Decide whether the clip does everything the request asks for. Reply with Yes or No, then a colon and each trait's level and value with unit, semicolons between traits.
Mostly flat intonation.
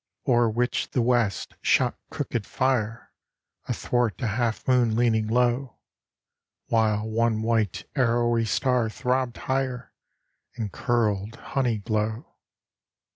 Yes: narrow, 2.1 semitones